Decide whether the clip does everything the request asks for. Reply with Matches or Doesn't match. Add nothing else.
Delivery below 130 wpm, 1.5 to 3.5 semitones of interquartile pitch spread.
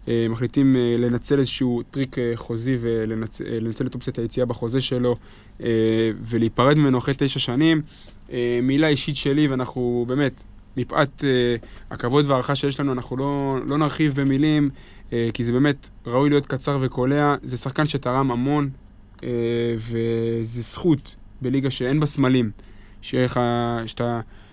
Matches